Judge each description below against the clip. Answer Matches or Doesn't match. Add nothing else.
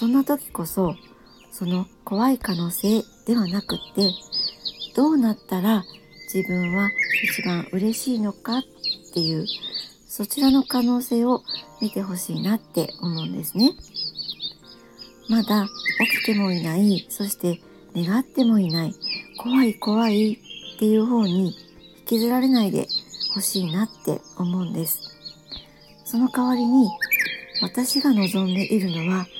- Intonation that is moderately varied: Matches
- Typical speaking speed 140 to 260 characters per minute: Matches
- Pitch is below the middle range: Doesn't match